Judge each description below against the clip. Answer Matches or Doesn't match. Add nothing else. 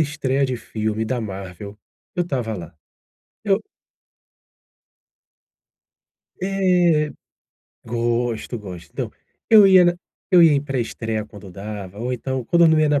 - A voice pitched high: Doesn't match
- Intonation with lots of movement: Matches